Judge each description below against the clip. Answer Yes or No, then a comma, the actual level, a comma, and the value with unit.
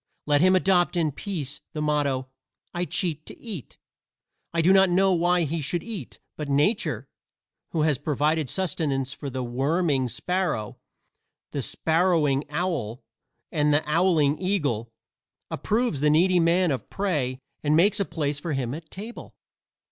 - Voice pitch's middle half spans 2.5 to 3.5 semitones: No, average, 4.2 semitones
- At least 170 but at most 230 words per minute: No, average, 150 wpm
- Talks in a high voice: No, medium, 160 Hz